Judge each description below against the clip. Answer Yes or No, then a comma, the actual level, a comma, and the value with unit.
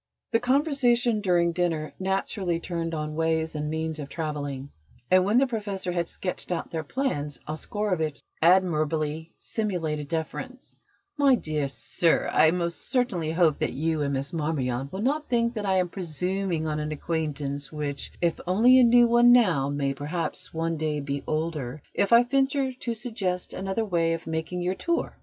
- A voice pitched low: No, medium, 170 Hz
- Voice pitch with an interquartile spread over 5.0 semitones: Yes, wide, 5.4 semitones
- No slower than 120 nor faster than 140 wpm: No, average, 175 wpm